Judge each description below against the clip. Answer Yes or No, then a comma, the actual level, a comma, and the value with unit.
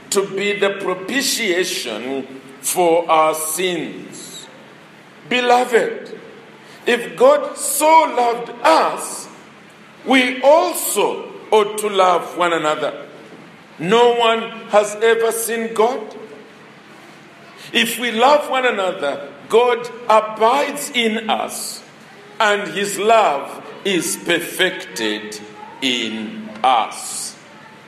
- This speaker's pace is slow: Yes, slow, 90 wpm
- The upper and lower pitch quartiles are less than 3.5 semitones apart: No, wide, 5.5 semitones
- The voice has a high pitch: Yes, high, 225 Hz